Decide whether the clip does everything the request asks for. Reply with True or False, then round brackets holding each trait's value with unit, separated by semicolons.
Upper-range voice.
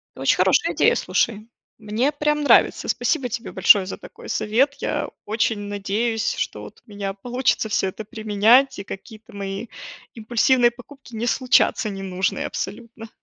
True (225 Hz)